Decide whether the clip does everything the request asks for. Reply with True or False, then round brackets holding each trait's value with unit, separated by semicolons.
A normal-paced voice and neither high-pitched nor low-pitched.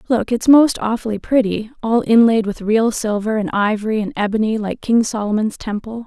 False (180 wpm; 220 Hz)